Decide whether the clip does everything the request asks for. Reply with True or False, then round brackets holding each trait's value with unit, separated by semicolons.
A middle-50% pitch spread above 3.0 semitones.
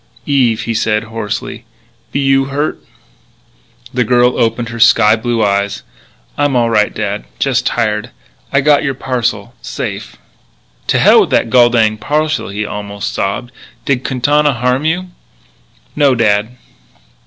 True (3.9 semitones)